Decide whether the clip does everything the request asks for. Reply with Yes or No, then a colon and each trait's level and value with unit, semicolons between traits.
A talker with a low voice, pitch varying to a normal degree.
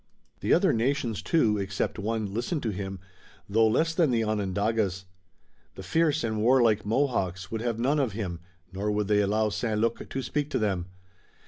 Yes: low, 110 Hz; average, 3.2 semitones